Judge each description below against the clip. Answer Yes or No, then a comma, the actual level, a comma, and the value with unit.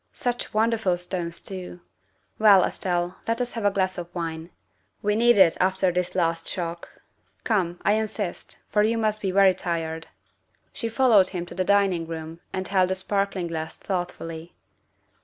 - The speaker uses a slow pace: No, average, 165 wpm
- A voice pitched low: No, medium, 185 Hz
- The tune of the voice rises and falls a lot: No, average, 3.2 semitones